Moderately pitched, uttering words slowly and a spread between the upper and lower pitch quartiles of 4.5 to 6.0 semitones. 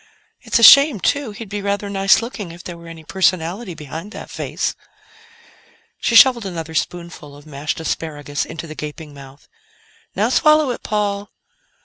No: medium, 175 Hz; average, 160 wpm; average, 4.9 semitones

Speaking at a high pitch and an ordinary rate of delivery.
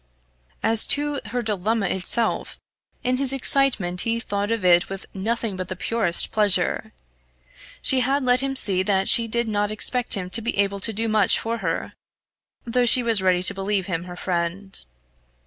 Yes: high, 215 Hz; average, 180 wpm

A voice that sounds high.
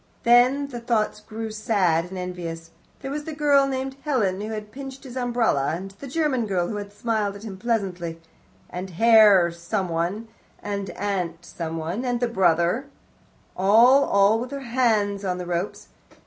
Yes: high, 210 Hz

